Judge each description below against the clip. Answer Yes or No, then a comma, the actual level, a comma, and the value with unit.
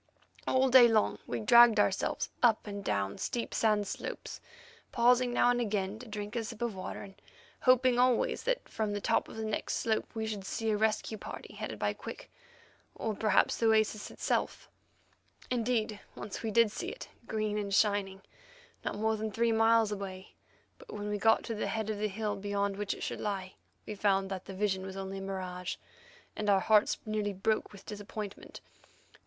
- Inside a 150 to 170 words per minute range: No, average, 190 wpm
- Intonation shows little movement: Yes, narrow, 2.0 semitones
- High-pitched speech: Yes, high, 215 Hz